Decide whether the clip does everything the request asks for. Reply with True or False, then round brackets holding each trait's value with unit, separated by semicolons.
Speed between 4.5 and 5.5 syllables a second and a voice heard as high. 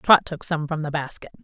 False (5.4 syllables/s; 155 Hz)